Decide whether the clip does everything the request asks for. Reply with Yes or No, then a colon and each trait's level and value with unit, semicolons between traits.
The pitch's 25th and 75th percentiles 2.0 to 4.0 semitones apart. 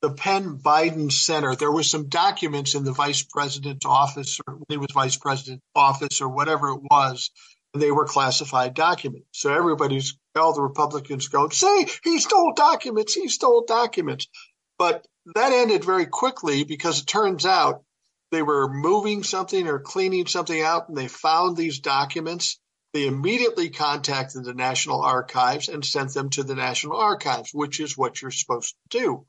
No: average, 4.7 semitones